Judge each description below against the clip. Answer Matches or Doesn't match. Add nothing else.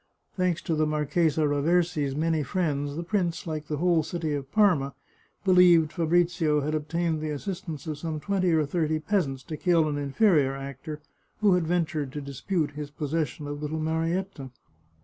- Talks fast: Doesn't match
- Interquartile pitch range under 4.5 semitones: Matches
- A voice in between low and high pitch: Matches